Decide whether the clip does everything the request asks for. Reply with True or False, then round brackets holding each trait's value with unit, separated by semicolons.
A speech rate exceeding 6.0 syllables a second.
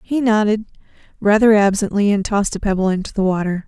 True (6.3 syllables/s)